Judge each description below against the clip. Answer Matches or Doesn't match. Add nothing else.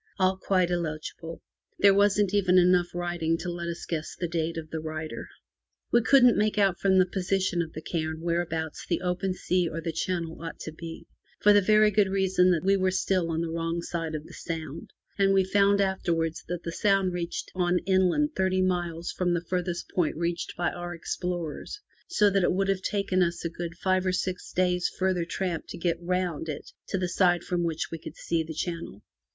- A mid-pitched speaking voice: Matches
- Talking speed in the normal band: Doesn't match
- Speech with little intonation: Matches